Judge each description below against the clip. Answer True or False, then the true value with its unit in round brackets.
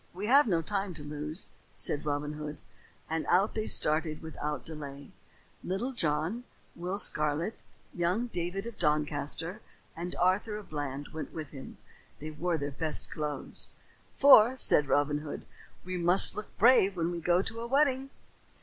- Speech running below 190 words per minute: True (160 wpm)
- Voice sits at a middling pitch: True (170 Hz)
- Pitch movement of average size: True (5.0 semitones)